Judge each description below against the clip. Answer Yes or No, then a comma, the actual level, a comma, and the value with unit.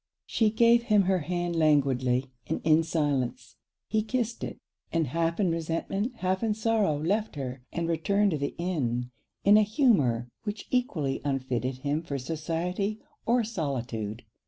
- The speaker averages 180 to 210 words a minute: No, average, 155 wpm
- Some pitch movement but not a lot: No, wide, 7.3 semitones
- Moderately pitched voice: Yes, medium, 165 Hz